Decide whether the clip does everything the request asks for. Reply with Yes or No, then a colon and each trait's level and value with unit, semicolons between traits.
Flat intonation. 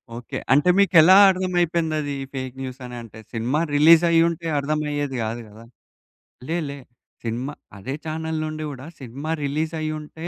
No: average, 3.7 semitones